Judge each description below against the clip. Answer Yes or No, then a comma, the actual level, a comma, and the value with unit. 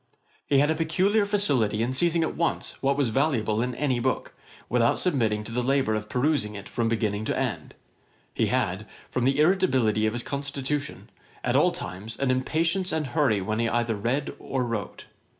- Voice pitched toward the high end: No, low, 130 Hz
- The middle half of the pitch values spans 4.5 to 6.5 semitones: Yes, average, 5.0 semitones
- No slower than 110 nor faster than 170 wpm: No, average, 185 wpm